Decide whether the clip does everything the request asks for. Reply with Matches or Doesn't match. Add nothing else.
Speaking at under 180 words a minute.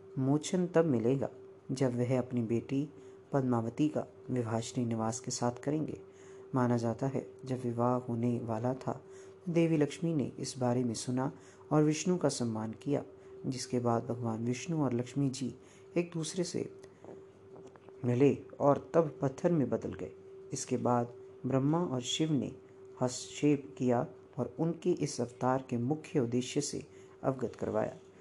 Matches